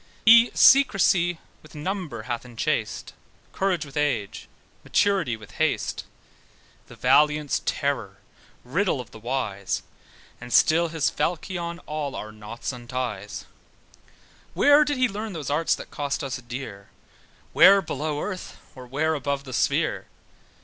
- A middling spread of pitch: No, wide, 6.2 semitones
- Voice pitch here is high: No, medium, 145 Hz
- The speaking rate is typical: No, slow, 130 wpm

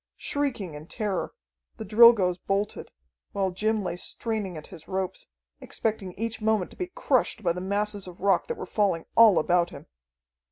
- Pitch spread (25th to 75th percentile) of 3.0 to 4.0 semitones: Yes, average, 3.4 semitones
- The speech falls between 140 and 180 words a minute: Yes, average, 170 wpm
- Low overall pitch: No, high, 200 Hz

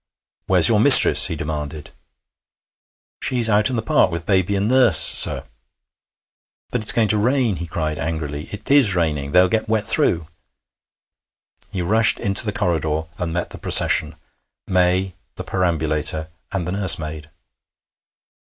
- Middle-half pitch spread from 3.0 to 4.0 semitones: No, average, 5.1 semitones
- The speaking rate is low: No, average, 145 wpm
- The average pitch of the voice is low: Yes, very low, 90 Hz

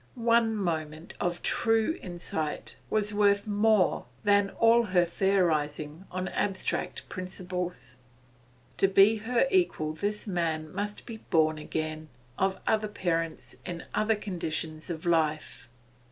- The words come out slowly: Yes, slow, 125 wpm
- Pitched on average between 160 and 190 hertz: Yes, medium, 185 Hz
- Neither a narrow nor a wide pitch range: Yes, average, 4.7 semitones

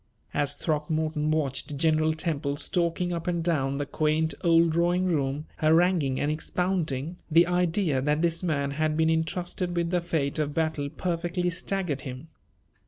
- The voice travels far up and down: No, average, 2.7 semitones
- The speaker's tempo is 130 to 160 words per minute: Yes, average, 155 wpm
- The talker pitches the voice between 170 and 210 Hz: No, medium, 160 Hz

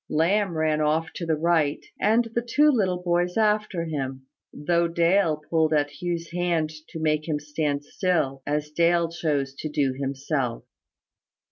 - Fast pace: No, average, 155 wpm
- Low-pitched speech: No, medium, 160 Hz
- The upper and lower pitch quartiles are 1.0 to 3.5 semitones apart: Yes, average, 2.9 semitones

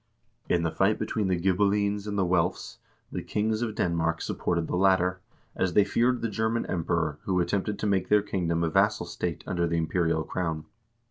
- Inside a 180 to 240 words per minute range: Yes, average, 195 wpm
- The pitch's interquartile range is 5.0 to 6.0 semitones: No, average, 3.5 semitones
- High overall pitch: No, very low, 95 Hz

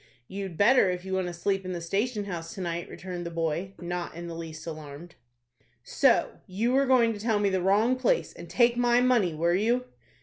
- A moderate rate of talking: No, fast, 215 wpm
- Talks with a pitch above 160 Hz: Yes, high, 190 Hz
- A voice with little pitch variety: No, average, 5.0 semitones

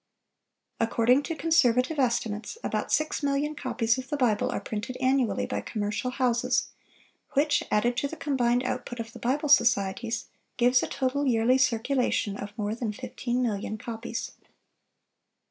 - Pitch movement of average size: Yes, average, 3.2 semitones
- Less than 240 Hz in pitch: No, high, 245 Hz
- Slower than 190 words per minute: Yes, average, 145 wpm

